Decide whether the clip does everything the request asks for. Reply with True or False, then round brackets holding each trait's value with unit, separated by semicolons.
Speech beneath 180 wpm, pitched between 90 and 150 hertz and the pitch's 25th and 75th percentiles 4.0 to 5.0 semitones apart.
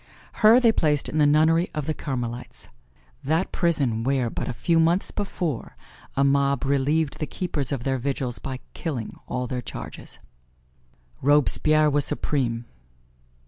False (145 wpm; 140 Hz; 3.4 semitones)